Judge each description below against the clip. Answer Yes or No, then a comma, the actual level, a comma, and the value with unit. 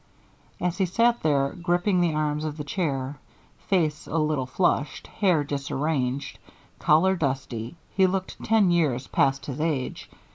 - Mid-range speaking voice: Yes, medium, 155 Hz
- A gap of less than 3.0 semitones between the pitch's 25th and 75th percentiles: No, average, 4.4 semitones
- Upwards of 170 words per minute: No, average, 145 wpm